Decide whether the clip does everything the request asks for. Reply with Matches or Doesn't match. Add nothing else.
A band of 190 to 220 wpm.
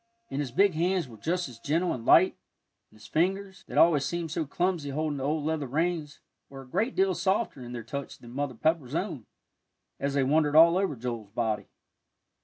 Matches